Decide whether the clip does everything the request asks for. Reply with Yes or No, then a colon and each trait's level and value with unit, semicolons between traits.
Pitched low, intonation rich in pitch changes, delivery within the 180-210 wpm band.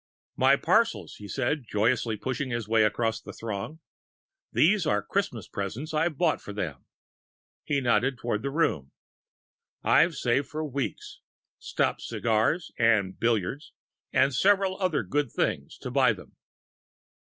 No: low, 130 Hz; wide, 5.9 semitones; average, 140 wpm